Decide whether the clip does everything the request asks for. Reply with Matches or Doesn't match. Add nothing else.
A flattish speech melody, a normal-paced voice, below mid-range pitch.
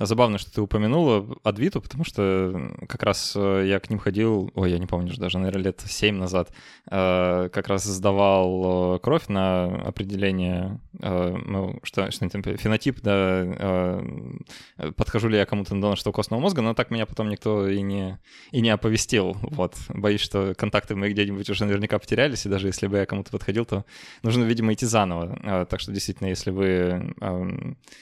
Doesn't match